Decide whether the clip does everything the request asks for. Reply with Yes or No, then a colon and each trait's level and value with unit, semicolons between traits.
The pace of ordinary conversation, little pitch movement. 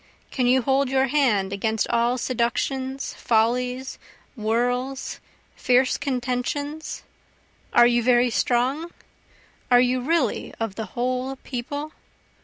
No: slow, 110 wpm; narrow, 1.9 semitones